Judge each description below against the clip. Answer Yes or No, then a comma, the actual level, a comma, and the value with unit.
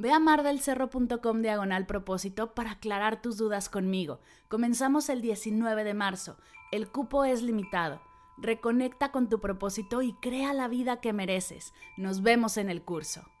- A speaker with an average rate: Yes, average, 150 wpm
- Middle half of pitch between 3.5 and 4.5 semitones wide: Yes, average, 4.2 semitones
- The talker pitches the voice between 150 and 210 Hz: No, high, 220 Hz